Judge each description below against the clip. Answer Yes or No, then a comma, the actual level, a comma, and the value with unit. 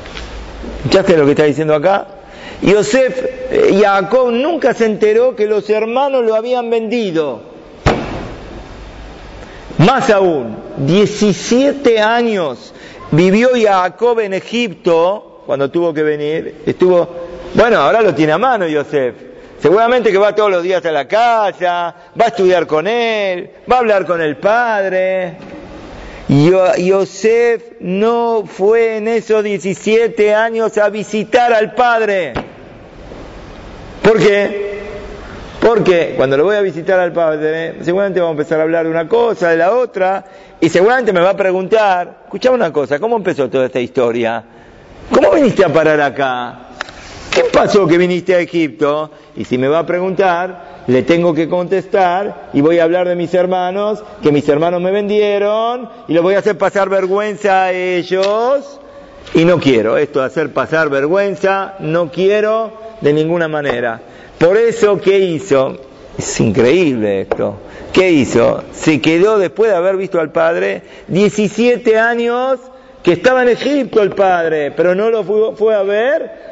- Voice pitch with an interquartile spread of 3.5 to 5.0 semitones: Yes, average, 4.6 semitones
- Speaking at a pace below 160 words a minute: Yes, average, 150 wpm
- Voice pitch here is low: No, high, 195 Hz